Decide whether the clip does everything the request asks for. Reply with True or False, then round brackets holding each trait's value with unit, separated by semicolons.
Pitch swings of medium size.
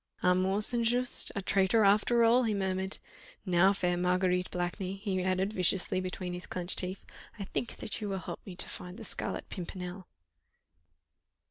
False (2.0 semitones)